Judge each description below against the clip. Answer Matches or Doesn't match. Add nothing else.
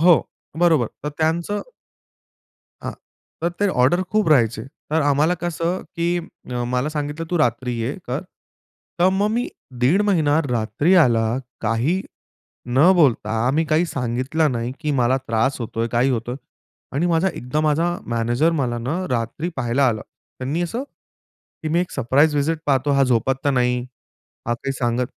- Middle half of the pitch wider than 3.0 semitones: Matches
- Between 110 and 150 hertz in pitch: Matches